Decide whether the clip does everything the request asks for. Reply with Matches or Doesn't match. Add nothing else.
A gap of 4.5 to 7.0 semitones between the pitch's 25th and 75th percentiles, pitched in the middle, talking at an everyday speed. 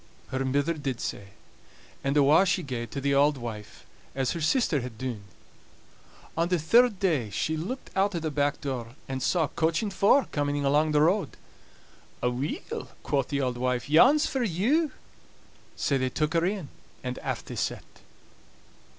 Matches